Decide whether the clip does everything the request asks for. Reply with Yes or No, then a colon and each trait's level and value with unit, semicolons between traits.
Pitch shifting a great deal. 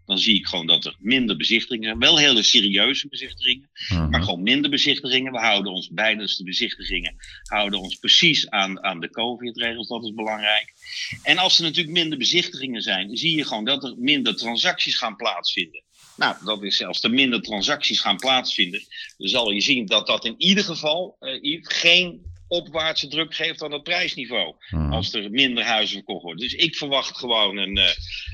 Yes: wide, 8.0 semitones